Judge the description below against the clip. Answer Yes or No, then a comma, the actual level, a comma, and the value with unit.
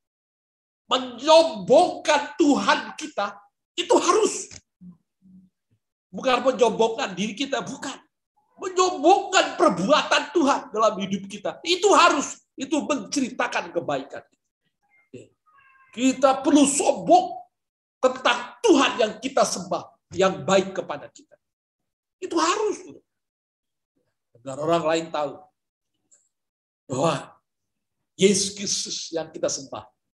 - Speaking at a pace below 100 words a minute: Yes, average, 90 wpm